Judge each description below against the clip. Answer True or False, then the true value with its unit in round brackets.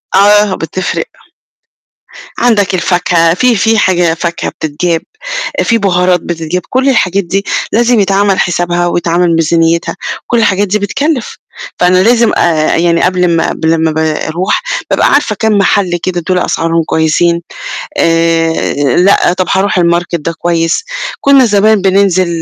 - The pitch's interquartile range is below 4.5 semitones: True (3.2 semitones)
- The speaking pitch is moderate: True (180 Hz)